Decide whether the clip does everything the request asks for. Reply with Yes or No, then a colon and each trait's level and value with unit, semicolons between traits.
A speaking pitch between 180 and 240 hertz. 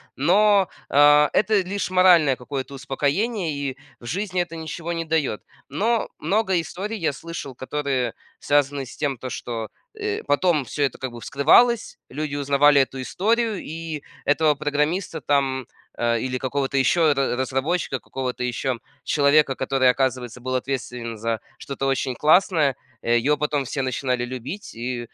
No: medium, 140 Hz